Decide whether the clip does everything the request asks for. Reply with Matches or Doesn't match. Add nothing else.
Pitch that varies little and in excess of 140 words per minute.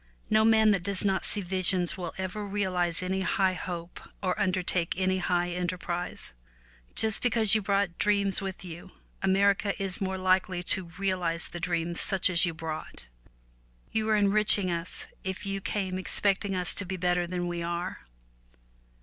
Matches